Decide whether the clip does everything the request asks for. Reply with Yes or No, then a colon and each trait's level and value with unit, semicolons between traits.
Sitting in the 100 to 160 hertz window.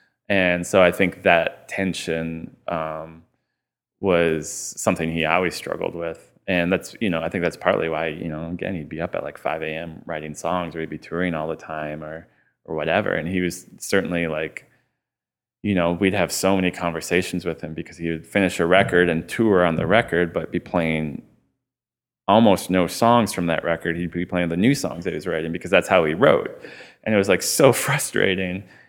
No: very low, 85 Hz